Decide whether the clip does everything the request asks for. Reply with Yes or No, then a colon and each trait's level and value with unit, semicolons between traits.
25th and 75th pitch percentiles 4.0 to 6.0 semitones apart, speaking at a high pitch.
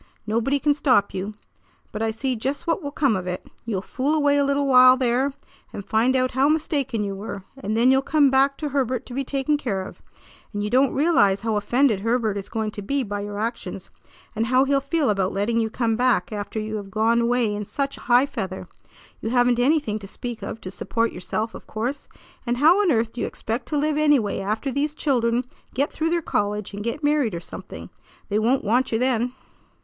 Yes: average, 4.4 semitones; high, 245 Hz